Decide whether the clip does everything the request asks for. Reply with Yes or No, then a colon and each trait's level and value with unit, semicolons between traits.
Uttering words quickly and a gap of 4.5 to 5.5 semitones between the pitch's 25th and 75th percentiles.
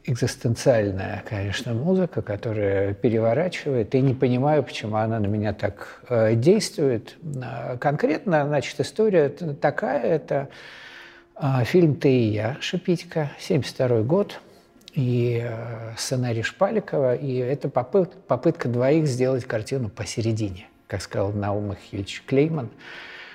No: slow, 110 wpm; average, 5.0 semitones